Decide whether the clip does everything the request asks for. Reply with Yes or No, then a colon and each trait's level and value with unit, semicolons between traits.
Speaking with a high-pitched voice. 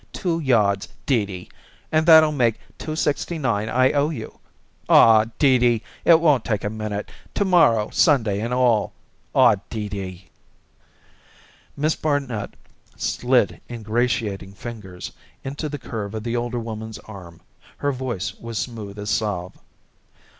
No: low, 115 Hz